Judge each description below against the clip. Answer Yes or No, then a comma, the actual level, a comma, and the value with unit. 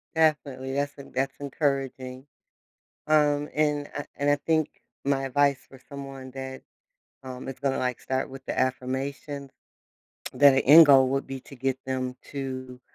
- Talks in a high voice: No, low, 135 Hz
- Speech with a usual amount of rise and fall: No, narrow, 1.6 semitones